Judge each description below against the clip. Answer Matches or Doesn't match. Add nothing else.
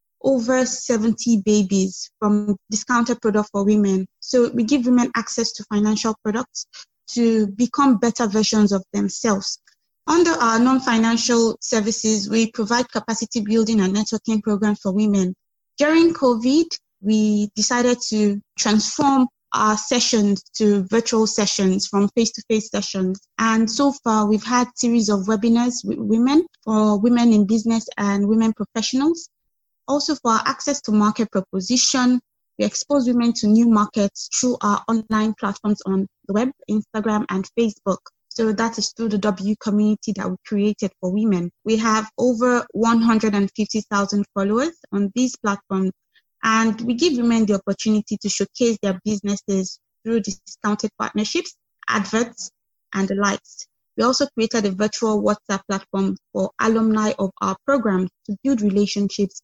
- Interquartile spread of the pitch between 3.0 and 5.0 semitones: Doesn't match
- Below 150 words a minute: Matches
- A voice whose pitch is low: Doesn't match